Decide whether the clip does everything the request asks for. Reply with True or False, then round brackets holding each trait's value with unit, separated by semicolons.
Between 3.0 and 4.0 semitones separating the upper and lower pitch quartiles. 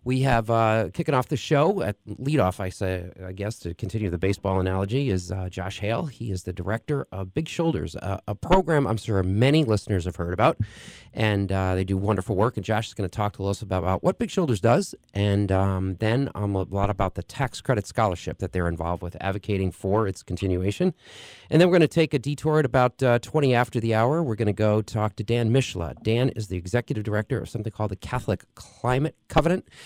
False (4.8 semitones)